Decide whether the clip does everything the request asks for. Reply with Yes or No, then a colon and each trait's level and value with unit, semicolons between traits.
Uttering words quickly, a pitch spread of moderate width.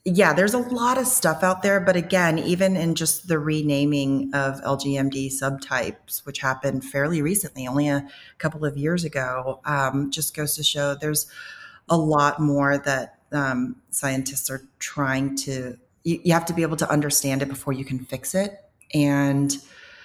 No: average, 175 wpm; average, 3.2 semitones